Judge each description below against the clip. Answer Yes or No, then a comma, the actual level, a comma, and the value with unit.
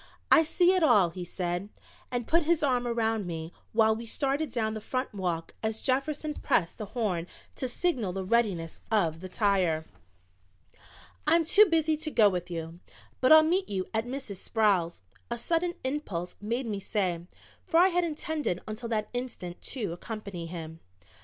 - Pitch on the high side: Yes, high, 220 Hz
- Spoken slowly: No, average, 170 wpm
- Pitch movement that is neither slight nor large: No, wide, 7.6 semitones